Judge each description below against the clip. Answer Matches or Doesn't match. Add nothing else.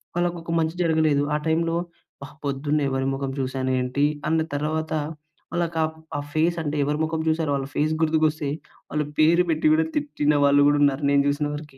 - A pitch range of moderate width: Doesn't match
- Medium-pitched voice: Matches